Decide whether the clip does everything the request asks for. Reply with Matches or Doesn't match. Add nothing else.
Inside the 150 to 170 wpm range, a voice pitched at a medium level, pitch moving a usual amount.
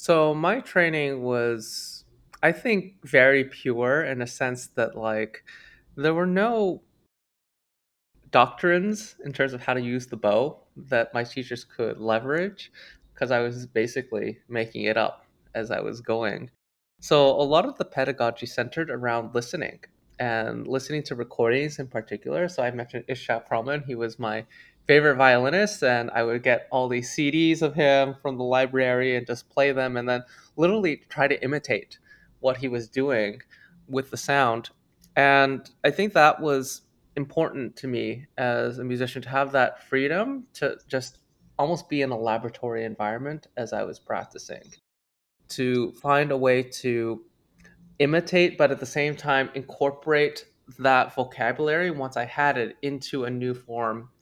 Doesn't match